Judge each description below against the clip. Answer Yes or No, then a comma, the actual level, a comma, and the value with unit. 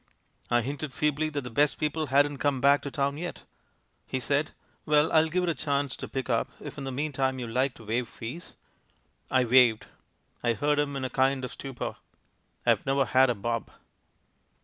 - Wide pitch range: No, narrow, 2.5 semitones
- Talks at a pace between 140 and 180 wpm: No, average, 195 wpm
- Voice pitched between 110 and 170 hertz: Yes, low, 135 Hz